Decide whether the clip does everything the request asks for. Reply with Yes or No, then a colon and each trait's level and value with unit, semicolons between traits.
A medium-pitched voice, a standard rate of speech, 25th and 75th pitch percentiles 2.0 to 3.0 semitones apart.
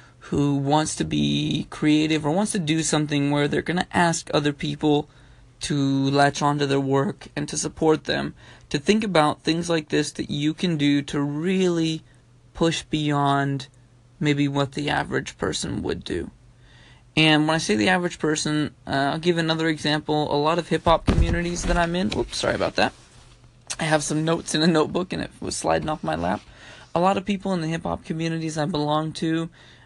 Yes: medium, 150 Hz; average, 195 wpm; average, 2.7 semitones